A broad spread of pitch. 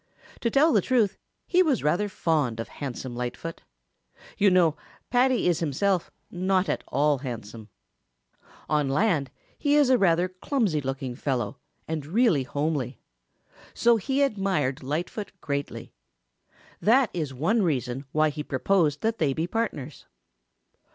Yes: wide, 7.0 semitones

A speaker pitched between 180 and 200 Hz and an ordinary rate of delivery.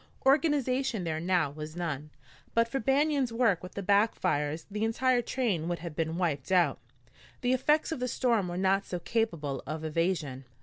Yes: high, 190 Hz; average, 180 wpm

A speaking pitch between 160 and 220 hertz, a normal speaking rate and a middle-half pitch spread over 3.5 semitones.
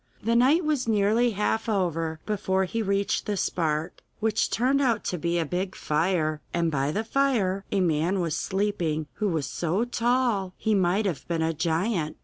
Yes: high, 190 Hz; average, 180 wpm; average, 5.0 semitones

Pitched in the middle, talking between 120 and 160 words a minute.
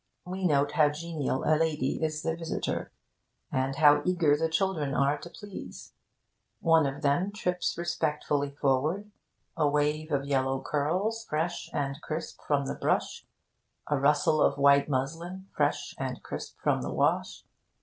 Yes: medium, 150 Hz; average, 150 wpm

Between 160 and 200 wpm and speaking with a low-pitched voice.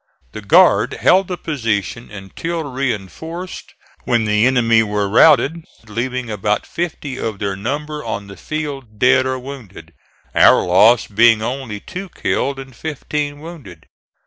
No: average, 140 wpm; low, 125 Hz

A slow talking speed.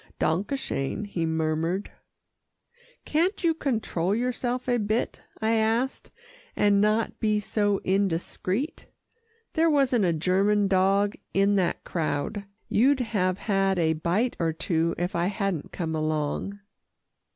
Yes: slow, 130 wpm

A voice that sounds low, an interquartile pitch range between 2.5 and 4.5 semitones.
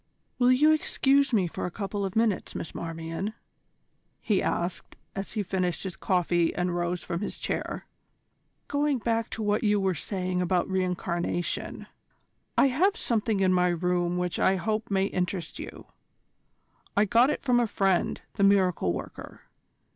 No: high, 190 Hz; average, 3.8 semitones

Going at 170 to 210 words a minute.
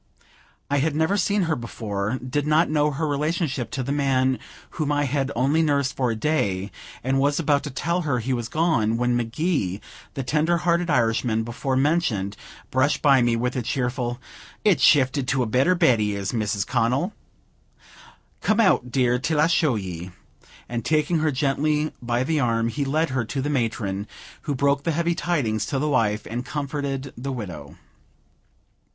Yes: average, 180 wpm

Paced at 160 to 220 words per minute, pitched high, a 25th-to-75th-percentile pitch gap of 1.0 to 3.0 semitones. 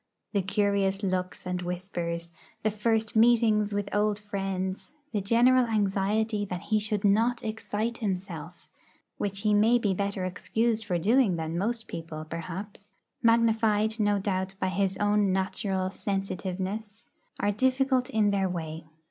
No: average, 140 wpm; high, 205 Hz; average, 2.7 semitones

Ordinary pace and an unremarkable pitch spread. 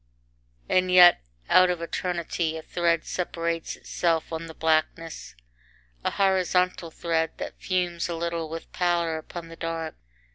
No: average, 145 wpm; narrow, 1.5 semitones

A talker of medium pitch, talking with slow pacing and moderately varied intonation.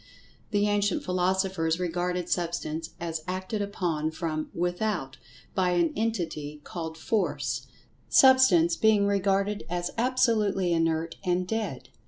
Yes: medium, 180 Hz; slow, 115 wpm; average, 3.6 semitones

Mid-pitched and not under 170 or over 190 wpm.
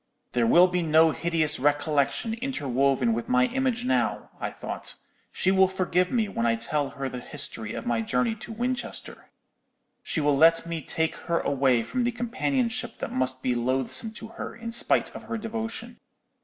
Yes: medium, 165 Hz; average, 180 wpm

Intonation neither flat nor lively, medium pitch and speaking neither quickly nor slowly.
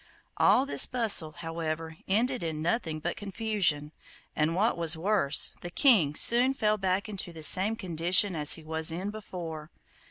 Yes: average, 4.9 semitones; medium, 175 Hz; average, 160 wpm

